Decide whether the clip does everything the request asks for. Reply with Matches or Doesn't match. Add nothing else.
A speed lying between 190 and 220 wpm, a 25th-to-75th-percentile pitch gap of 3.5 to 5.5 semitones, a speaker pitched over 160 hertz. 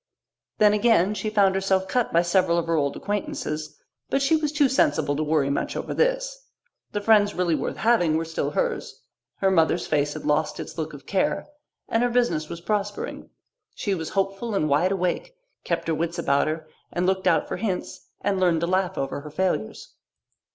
Matches